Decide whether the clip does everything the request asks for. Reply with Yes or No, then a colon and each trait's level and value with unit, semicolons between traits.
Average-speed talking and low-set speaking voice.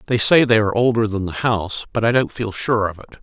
No: fast, 280 wpm; low, 110 Hz